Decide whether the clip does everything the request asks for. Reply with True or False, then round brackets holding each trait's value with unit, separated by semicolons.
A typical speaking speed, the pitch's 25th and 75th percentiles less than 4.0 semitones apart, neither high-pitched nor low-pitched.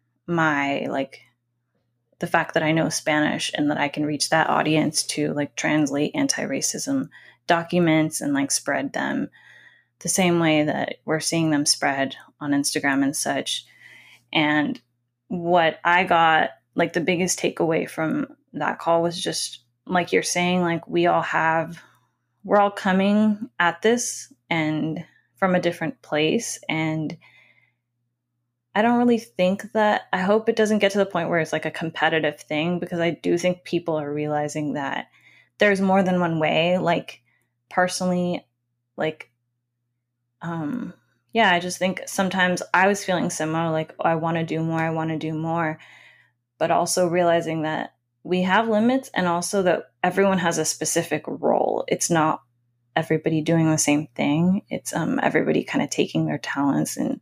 True (165 wpm; 3.3 semitones; 165 Hz)